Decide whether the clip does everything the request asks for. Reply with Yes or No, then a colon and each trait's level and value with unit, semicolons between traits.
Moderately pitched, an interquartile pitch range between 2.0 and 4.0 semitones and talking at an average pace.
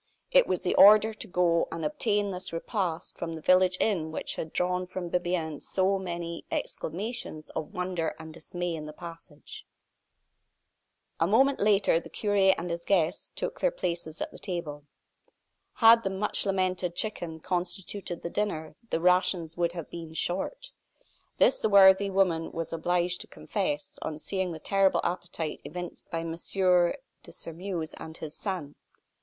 Yes: medium, 180 Hz; average, 2.8 semitones; average, 160 wpm